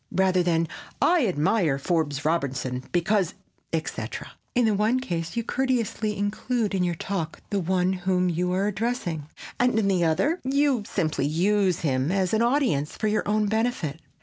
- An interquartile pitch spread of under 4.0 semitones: No, average, 5.0 semitones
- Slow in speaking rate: No, average, 165 wpm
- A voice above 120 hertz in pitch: Yes, high, 190 Hz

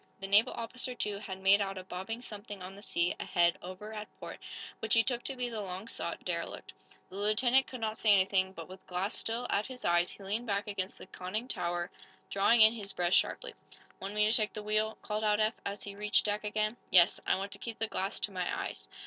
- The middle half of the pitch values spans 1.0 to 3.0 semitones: Yes, narrow, 2.5 semitones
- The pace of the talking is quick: Yes, fast, 235 wpm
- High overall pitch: Yes, high, 205 Hz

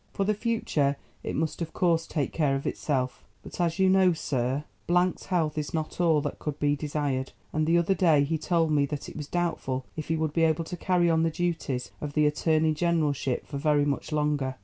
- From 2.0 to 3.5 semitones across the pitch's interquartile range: Yes, average, 2.8 semitones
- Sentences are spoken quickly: Yes, fast, 220 wpm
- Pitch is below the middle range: No, medium, 155 Hz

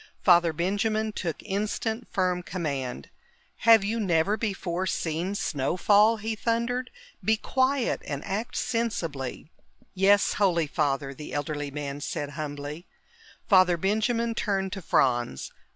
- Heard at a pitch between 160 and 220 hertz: Yes, medium, 185 Hz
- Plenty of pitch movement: Yes, wide, 6.2 semitones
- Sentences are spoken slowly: Yes, slow, 125 wpm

